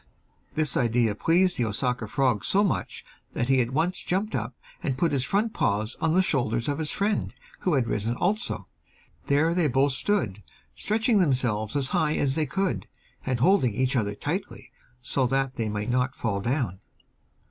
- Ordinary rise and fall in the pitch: No, wide, 6.3 semitones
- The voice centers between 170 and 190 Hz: No, low, 135 Hz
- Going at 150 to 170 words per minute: No, average, 180 wpm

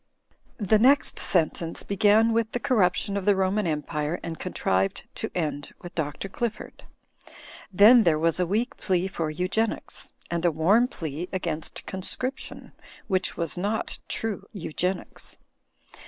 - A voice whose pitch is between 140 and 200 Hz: Yes, medium, 185 Hz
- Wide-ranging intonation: No, average, 4.3 semitones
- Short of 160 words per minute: Yes, average, 140 wpm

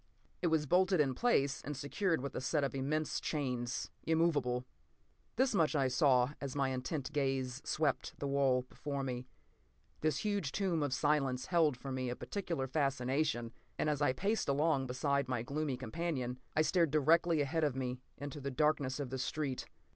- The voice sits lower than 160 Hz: Yes, medium, 140 Hz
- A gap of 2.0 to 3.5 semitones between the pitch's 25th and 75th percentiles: Yes, average, 3.2 semitones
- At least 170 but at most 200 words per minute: Yes, average, 175 wpm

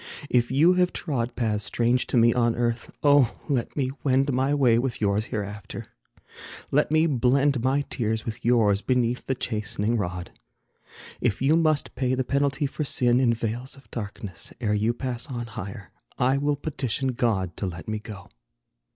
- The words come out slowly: No, average, 175 wpm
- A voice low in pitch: Yes, low, 120 Hz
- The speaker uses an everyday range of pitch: Yes, average, 3.6 semitones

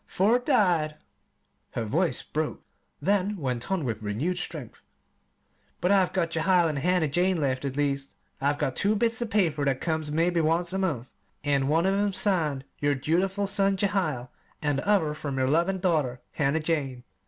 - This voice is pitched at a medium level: Yes, medium, 160 Hz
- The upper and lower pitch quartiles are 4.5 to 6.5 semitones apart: Yes, average, 5.2 semitones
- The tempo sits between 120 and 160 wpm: No, average, 175 wpm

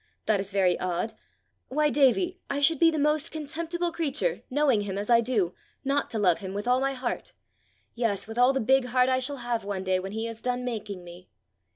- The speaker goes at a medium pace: No, fast, 220 wpm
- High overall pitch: Yes, high, 245 Hz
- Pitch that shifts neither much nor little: No, wide, 5.7 semitones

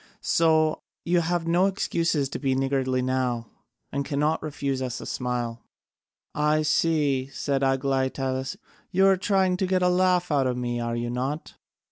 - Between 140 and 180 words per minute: Yes, average, 160 wpm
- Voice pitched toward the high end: No, medium, 140 Hz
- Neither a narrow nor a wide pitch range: Yes, average, 4.4 semitones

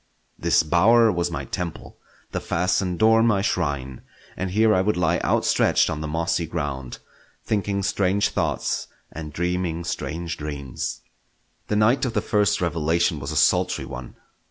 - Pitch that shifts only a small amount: No, average, 4.3 semitones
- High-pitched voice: No, very low, 90 Hz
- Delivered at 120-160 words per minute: Yes, average, 155 wpm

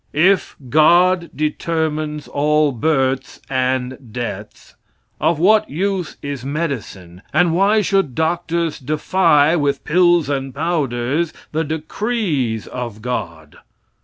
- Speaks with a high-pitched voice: No, medium, 150 Hz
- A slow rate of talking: Yes, slow, 105 wpm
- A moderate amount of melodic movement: Yes, average, 4.6 semitones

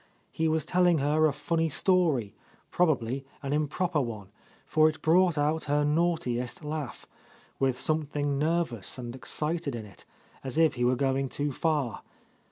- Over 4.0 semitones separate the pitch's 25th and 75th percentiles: No, average, 3.5 semitones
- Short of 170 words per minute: Yes, average, 155 wpm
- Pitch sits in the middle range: Yes, medium, 150 Hz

